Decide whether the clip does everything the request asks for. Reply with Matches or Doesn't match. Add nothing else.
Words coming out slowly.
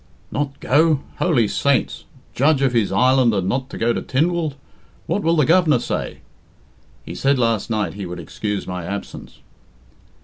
Doesn't match